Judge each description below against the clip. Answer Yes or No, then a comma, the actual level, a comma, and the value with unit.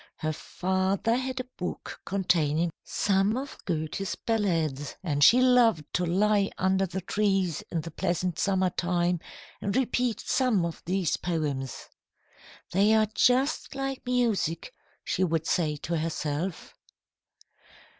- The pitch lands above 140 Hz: Yes, medium, 185 Hz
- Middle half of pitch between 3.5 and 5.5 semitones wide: Yes, average, 4.5 semitones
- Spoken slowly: Yes, slow, 130 wpm